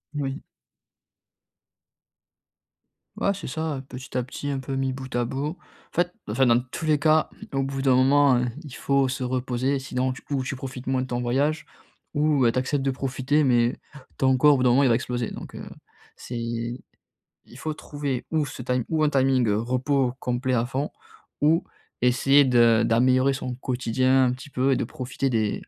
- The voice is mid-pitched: No, low, 130 Hz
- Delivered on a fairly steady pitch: Yes, narrow, 2.0 semitones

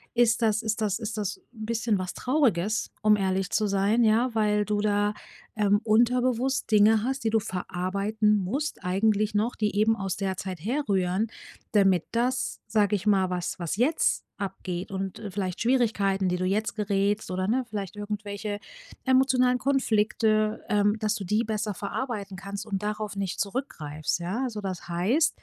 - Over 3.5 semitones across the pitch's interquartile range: No, narrow, 2.5 semitones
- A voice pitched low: No, high, 210 Hz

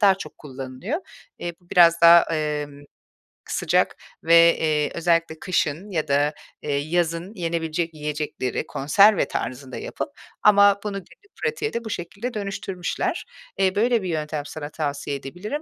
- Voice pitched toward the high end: No, medium, 170 Hz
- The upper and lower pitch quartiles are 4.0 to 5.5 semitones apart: Yes, average, 4.7 semitones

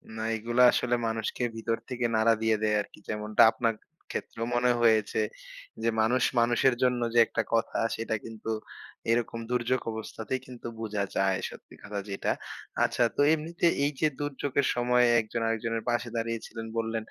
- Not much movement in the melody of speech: Yes, narrow, 1.7 semitones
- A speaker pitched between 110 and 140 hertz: Yes, low, 115 Hz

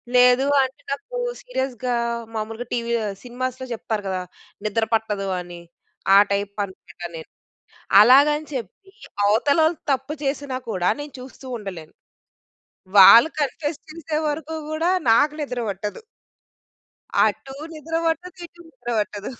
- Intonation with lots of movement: Yes, wide, 6.1 semitones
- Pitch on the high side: Yes, very high, 250 Hz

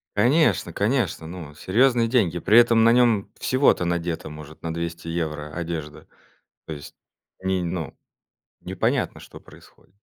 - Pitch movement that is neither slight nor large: No, wide, 6.0 semitones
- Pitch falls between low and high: No, very low, 85 Hz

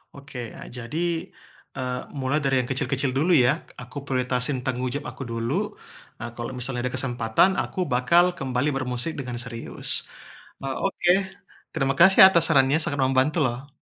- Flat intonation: Yes, narrow, 2.3 semitones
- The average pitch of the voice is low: Yes, low, 130 Hz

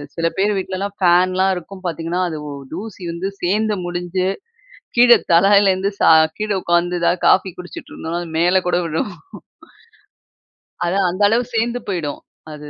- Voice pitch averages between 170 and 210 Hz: Yes, medium, 185 Hz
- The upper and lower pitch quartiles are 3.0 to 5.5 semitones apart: No, narrow, 2.6 semitones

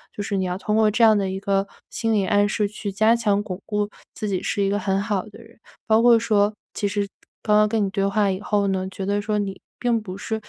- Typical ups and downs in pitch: No, narrow, 1.6 semitones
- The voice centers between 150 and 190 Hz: No, high, 205 Hz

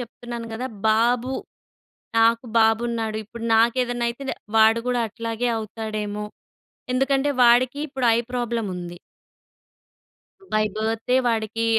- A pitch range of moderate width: No, narrow, 1.8 semitones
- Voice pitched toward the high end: Yes, high, 230 Hz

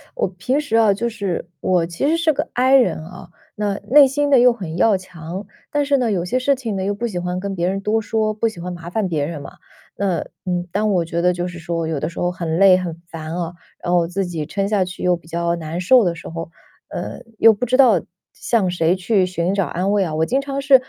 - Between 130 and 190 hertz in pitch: Yes, medium, 185 Hz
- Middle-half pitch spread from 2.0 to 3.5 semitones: No, average, 4.7 semitones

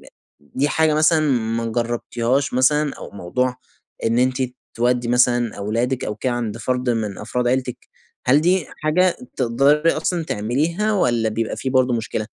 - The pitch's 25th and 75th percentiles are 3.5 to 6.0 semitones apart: Yes, average, 4.0 semitones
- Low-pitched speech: Yes, low, 125 Hz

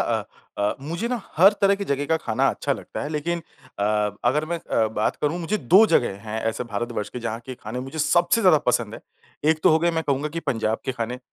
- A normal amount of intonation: No, wide, 6.4 semitones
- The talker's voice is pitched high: No, medium, 145 Hz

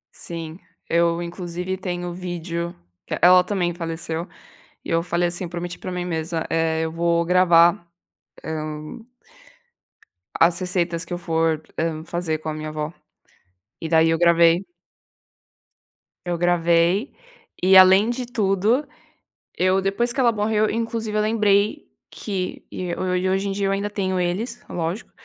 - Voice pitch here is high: No, medium, 175 Hz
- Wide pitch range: No, narrow, 2.6 semitones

